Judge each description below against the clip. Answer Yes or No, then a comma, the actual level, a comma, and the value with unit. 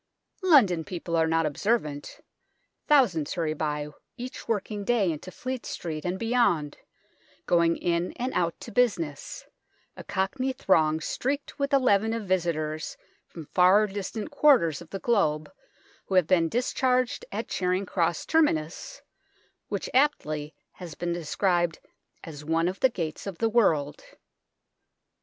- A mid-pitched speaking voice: Yes, medium, 180 Hz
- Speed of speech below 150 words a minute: Yes, average, 140 wpm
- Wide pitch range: Yes, wide, 6.3 semitones